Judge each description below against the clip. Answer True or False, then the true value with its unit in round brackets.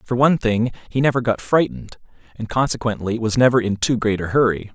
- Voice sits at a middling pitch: False (115 Hz)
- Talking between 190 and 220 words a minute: True (200 wpm)